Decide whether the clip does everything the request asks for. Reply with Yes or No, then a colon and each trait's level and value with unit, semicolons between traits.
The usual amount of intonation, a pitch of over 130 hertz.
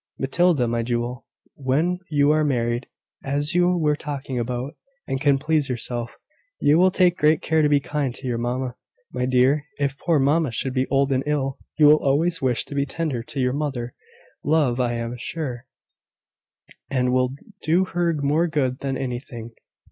Yes: average, 3.3 semitones; medium, 140 Hz